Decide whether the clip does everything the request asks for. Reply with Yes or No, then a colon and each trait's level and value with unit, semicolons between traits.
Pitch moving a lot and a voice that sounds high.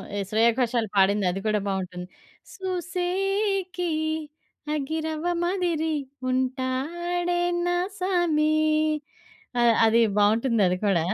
Yes: wide, 8.2 semitones; very high, 305 Hz